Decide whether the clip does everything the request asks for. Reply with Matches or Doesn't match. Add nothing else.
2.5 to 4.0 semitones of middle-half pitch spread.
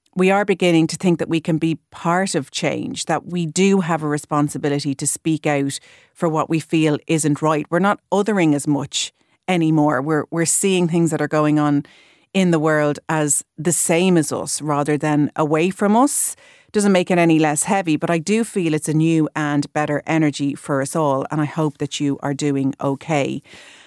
Matches